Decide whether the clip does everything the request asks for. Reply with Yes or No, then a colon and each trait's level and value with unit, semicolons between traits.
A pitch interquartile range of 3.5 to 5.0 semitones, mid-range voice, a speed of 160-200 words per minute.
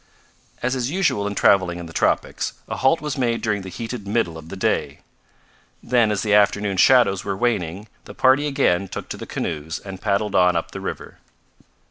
No: average, 4.6 semitones; low, 105 Hz; average, 195 wpm